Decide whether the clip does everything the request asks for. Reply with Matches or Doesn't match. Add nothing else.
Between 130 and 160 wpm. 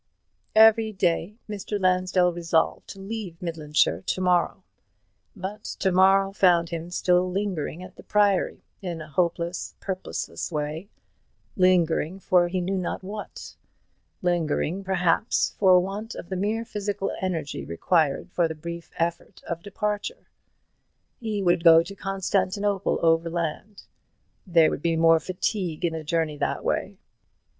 Matches